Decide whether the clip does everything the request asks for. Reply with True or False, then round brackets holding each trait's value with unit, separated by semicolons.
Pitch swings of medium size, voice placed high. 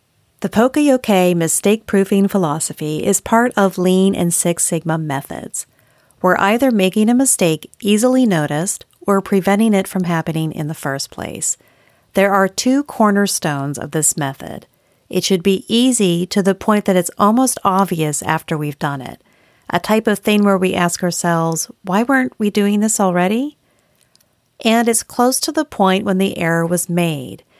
True (4.1 semitones; 195 Hz)